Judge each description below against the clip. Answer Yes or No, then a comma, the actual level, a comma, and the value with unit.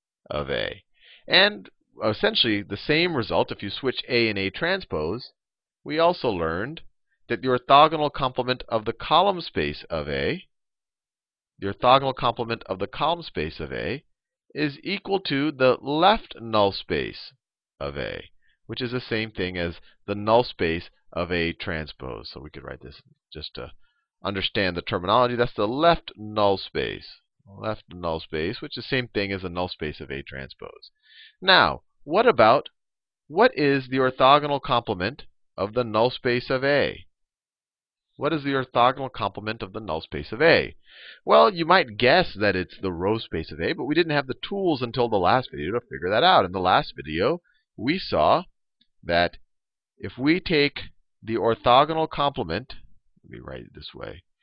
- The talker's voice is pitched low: Yes, low, 120 Hz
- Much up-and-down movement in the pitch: Yes, wide, 6.2 semitones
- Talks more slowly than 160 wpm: No, average, 175 wpm